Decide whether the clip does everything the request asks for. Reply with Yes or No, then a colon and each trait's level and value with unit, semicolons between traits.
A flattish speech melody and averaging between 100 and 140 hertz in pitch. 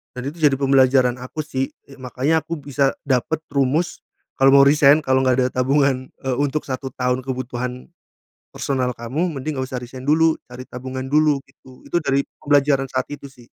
Yes: narrow, 2.1 semitones; low, 135 Hz